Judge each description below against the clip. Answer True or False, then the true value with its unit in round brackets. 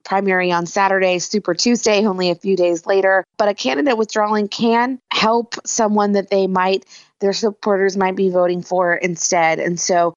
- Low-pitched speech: False (195 Hz)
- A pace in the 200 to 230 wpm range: False (170 wpm)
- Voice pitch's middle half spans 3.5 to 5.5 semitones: False (2.7 semitones)